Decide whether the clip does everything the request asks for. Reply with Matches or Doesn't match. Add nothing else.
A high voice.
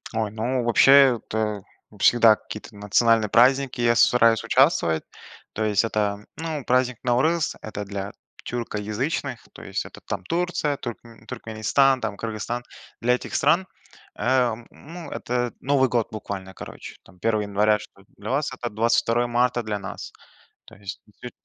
Doesn't match